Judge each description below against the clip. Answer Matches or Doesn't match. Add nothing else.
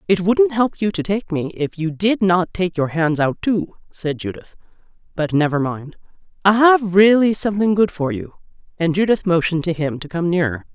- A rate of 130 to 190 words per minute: Doesn't match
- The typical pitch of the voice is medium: Matches